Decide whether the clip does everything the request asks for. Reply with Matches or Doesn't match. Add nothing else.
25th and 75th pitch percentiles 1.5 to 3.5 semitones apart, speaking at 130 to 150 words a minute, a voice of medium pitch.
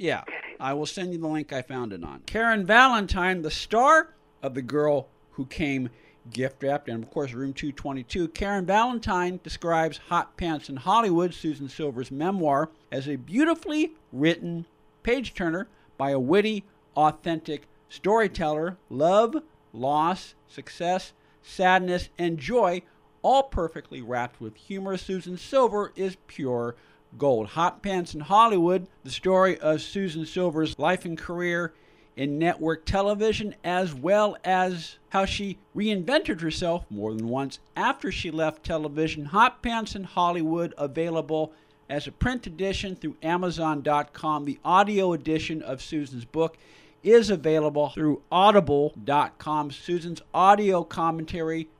Doesn't match